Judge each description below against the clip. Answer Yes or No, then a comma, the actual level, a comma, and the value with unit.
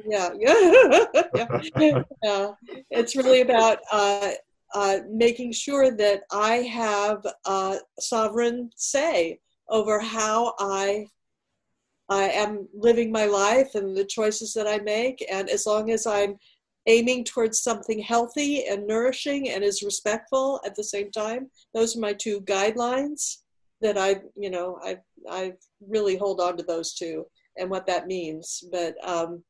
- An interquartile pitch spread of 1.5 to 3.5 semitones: Yes, average, 2.9 semitones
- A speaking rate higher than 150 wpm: No, average, 145 wpm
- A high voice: Yes, high, 215 Hz